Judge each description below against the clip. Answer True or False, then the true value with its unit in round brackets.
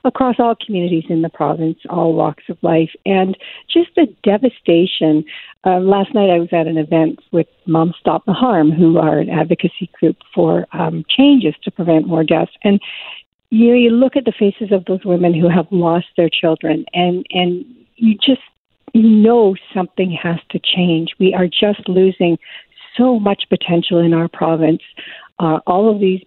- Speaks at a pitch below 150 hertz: False (180 Hz)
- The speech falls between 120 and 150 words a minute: False (180 wpm)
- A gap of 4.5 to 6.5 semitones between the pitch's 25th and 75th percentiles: False (3.8 semitones)